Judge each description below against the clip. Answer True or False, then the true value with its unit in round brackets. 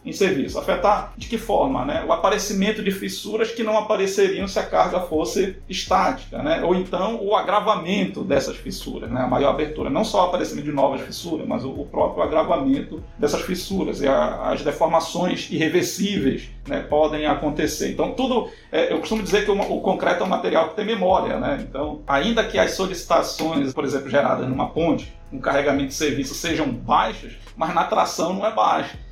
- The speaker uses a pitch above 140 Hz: True (190 Hz)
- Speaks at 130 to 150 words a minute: False (180 wpm)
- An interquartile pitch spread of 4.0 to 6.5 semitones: True (5.2 semitones)